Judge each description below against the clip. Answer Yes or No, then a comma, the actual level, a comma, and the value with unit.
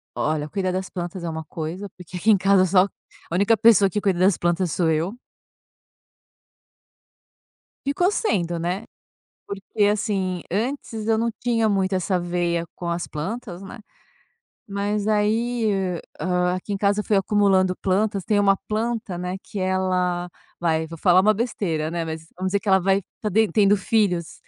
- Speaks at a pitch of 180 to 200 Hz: Yes, high, 190 Hz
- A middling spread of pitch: Yes, average, 3.0 semitones